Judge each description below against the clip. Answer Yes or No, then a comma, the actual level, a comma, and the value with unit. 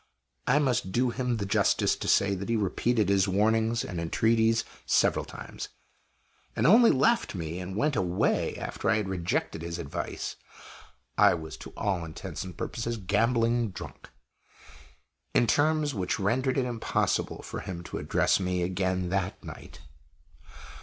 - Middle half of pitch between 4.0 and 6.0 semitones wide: Yes, average, 4.4 semitones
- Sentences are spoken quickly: No, average, 155 wpm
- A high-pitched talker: No, low, 105 Hz